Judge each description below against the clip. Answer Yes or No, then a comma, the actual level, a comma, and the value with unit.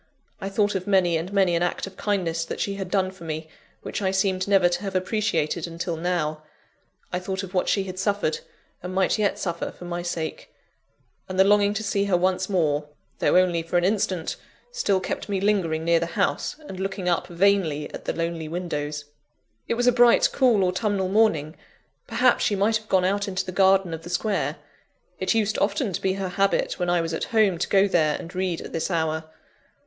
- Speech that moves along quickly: Yes, fast, 215 wpm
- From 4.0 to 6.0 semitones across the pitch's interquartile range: No, average, 2.9 semitones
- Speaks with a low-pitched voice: No, medium, 185 Hz